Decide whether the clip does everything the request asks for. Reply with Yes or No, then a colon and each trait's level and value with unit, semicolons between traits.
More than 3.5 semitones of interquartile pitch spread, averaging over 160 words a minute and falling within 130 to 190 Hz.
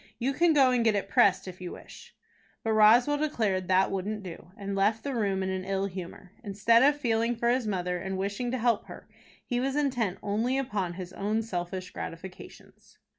No: average, 4.2 semitones; average, 200 wpm; high, 205 Hz